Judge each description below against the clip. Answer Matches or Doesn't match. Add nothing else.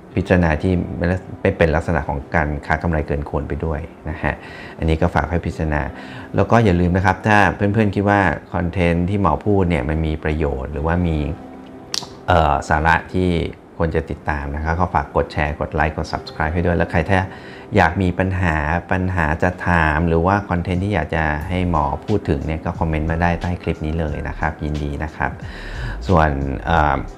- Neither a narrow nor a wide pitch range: Matches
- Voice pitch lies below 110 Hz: Matches